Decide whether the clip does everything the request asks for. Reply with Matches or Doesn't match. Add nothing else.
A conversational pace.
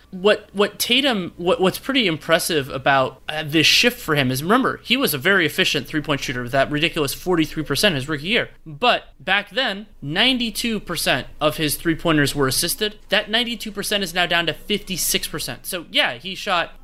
Matches